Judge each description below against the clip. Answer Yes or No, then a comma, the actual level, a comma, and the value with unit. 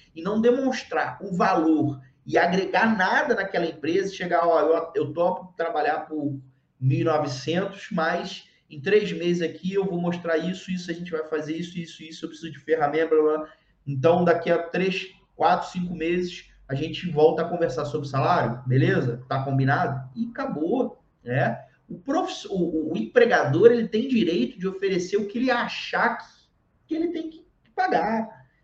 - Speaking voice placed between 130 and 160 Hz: No, medium, 170 Hz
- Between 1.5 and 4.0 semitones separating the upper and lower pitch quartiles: Yes, average, 3.7 semitones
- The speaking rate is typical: Yes, average, 175 wpm